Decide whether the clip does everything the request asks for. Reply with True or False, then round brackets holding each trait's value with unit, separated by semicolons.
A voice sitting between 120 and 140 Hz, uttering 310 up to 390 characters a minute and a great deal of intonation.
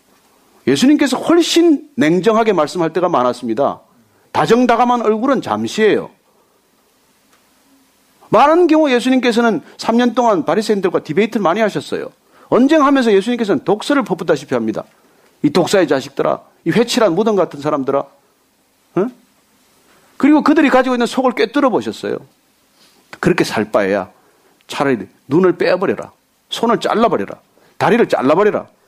False (240 Hz; 325 characters per minute; 5.9 semitones)